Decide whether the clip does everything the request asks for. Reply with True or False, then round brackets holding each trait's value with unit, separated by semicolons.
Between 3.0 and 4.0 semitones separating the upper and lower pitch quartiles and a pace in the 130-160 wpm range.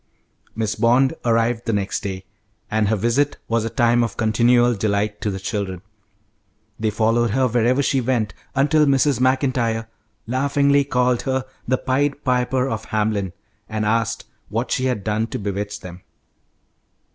True (3.3 semitones; 155 wpm)